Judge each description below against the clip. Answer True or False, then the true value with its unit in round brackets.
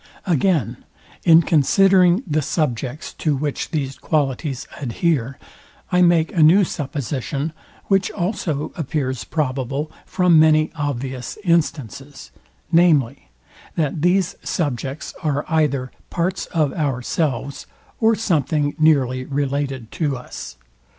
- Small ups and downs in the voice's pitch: False (3.8 semitones)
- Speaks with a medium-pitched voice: True (150 Hz)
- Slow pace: True (110 wpm)